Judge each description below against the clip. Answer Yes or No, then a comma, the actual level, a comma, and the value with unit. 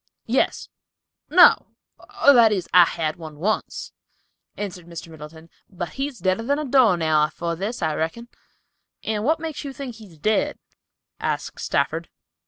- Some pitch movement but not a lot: No, wide, 6.9 semitones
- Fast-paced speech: No, average, 155 wpm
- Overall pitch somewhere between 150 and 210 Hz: Yes, high, 190 Hz